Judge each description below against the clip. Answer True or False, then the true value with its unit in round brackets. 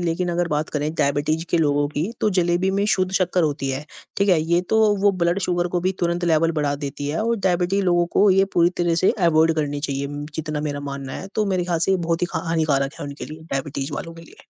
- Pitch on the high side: False (170 Hz)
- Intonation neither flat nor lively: True (3.4 semitones)